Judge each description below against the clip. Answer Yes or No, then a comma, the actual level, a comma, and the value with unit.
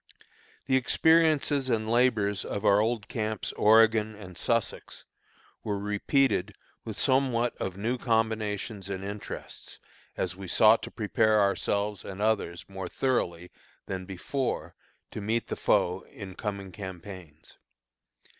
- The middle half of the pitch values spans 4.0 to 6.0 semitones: No, average, 2.9 semitones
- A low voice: Yes, low, 105 Hz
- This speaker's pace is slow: Yes, slow, 125 wpm